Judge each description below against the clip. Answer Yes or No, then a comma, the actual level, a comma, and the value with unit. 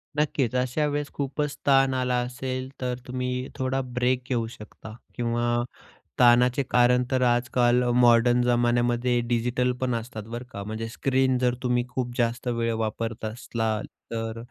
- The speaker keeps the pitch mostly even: Yes, narrow, 1.4 semitones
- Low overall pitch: Yes, low, 125 Hz